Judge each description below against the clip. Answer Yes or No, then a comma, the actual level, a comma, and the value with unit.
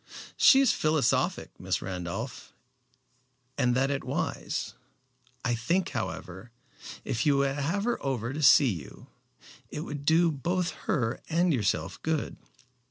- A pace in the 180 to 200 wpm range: No, slow, 135 wpm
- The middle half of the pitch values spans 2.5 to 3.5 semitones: No, wide, 5.5 semitones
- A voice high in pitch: No, medium, 140 Hz